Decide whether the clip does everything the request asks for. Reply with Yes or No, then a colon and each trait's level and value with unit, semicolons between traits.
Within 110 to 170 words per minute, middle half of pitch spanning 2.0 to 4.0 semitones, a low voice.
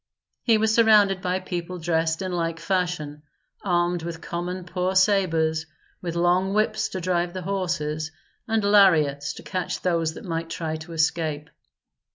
No: average, 155 wpm; narrow, 2.5 semitones; medium, 175 Hz